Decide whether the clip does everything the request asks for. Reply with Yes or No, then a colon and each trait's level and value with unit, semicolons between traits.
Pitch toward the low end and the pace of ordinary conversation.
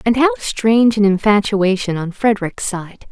No: high, 205 Hz; average, 155 wpm